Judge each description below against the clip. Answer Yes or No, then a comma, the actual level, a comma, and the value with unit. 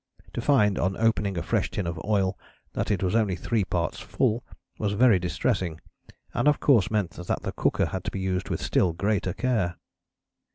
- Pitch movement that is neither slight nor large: Yes, average, 3.4 semitones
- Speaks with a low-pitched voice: Yes, low, 100 Hz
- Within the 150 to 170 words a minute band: No, average, 195 wpm